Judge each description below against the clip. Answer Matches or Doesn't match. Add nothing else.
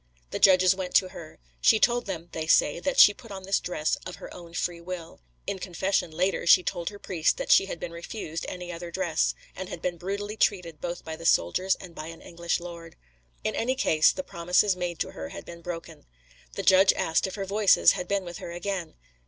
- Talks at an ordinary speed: Doesn't match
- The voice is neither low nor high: Matches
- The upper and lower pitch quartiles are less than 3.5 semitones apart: Matches